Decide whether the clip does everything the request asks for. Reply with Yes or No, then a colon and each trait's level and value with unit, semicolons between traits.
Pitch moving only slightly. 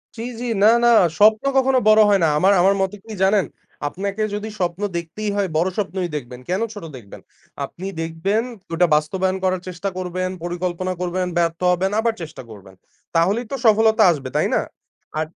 No: average, 3.5 semitones